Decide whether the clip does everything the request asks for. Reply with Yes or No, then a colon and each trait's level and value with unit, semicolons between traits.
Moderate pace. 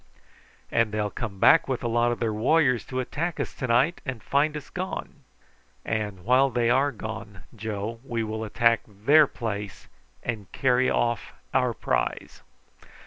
Yes: average, 160 wpm